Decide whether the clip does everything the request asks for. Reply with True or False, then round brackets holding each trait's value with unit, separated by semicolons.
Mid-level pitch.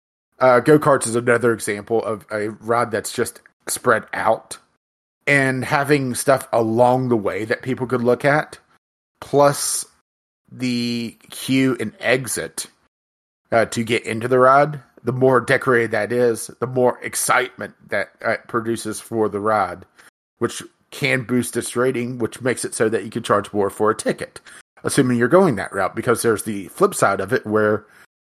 False (120 Hz)